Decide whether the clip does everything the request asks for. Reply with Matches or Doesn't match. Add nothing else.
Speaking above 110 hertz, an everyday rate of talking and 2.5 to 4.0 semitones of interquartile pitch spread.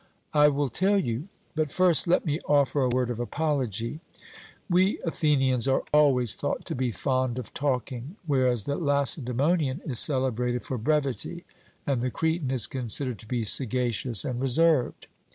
Matches